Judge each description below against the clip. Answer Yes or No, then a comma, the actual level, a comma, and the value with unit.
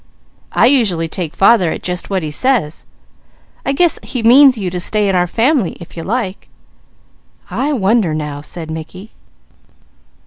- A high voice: Yes, high, 195 Hz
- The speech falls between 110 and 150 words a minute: No, average, 160 wpm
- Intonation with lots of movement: Yes, wide, 6.2 semitones